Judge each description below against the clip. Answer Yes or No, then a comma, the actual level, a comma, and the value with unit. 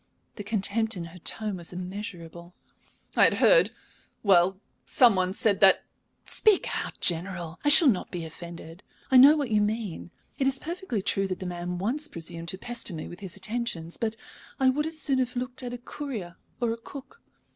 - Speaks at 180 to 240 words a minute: Yes, average, 195 wpm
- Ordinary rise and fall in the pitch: No, wide, 6.0 semitones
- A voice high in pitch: Yes, high, 205 Hz